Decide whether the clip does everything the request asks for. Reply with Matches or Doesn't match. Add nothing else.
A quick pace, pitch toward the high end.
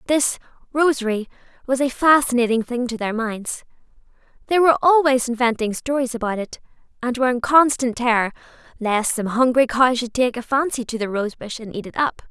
Doesn't match